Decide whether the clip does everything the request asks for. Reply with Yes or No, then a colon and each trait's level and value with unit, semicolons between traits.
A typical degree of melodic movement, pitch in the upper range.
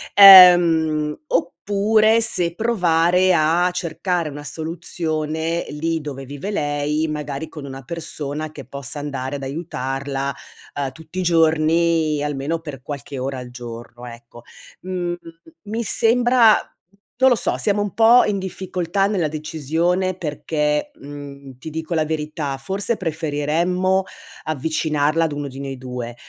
No: average, 3.8 semitones; medium, 160 Hz